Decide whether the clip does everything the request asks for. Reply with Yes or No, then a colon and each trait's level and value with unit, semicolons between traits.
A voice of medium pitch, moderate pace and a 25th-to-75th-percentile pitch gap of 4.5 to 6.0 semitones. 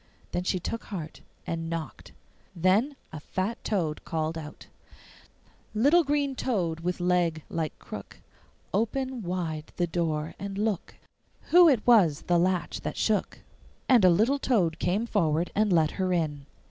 Yes: medium, 180 Hz; average, 150 wpm; average, 5.1 semitones